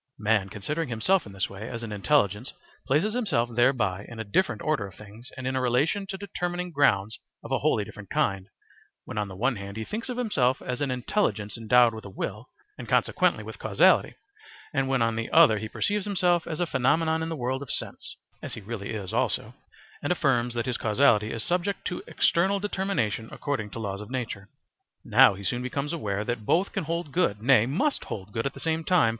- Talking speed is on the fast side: Yes, fast, 215 wpm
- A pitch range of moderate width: No, wide, 7.2 semitones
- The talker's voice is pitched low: Yes, low, 125 Hz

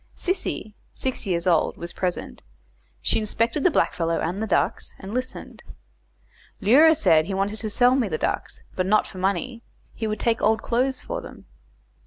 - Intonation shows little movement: No, average, 5.0 semitones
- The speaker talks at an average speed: Yes, average, 175 wpm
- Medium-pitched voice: No, high, 215 Hz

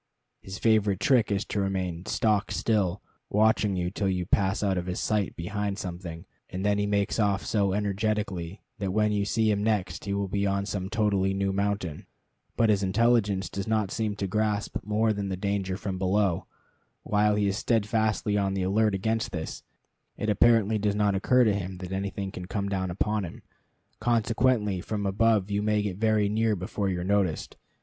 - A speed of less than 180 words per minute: No, average, 190 wpm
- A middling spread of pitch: No, narrow, 1.9 semitones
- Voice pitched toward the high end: No, low, 100 Hz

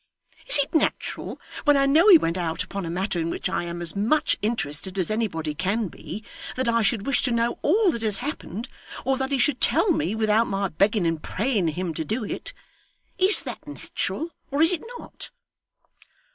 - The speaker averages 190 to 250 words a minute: Yes, average, 200 wpm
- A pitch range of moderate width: No, wide, 7.3 semitones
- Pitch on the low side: No, high, 220 Hz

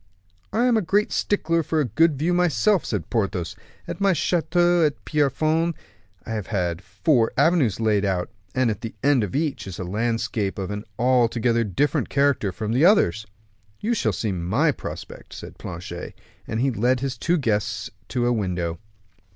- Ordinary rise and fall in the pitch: No, wide, 7.3 semitones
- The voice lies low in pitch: Yes, low, 120 Hz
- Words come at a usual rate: Yes, average, 175 wpm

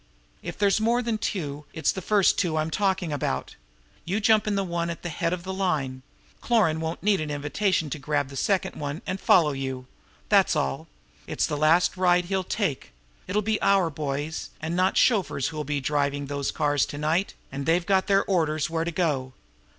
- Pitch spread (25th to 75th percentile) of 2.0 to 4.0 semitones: No, average, 4.6 semitones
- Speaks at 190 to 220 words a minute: Yes, average, 200 wpm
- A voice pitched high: No, medium, 165 Hz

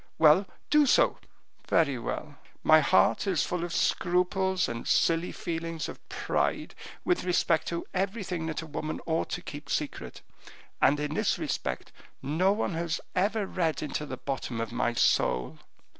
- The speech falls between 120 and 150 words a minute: No, average, 160 wpm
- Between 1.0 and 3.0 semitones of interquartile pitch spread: No, average, 3.8 semitones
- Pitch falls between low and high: Yes, medium, 165 Hz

